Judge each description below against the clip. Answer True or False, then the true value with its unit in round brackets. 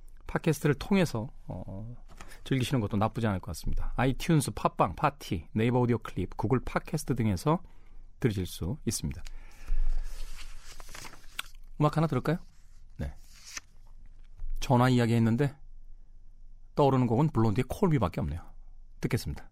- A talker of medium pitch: False (110 Hz)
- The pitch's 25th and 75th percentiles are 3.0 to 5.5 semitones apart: True (5.2 semitones)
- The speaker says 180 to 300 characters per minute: True (295 characters per minute)